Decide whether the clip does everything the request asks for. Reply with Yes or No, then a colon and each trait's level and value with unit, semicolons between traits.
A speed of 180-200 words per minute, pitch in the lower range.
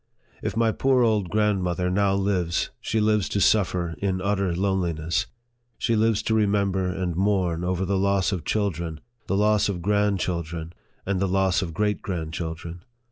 No: average, 165 wpm; very low, 95 Hz